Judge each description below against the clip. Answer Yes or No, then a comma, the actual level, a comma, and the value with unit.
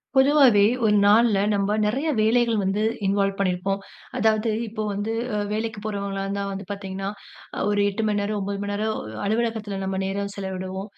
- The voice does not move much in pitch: Yes, narrow, 1.8 semitones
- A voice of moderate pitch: No, high, 205 Hz